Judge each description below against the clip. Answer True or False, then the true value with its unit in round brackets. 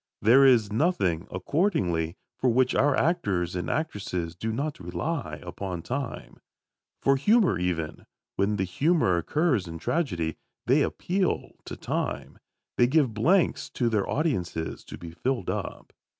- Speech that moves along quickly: False (140 wpm)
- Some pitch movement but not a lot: False (8.8 semitones)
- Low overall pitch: True (110 Hz)